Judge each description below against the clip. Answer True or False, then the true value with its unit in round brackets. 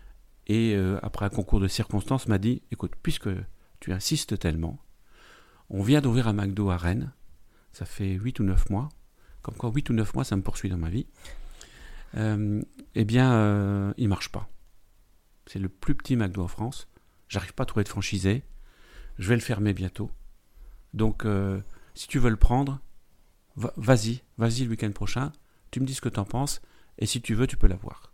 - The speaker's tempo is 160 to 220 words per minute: True (200 wpm)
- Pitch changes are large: False (4.0 semitones)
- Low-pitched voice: True (105 Hz)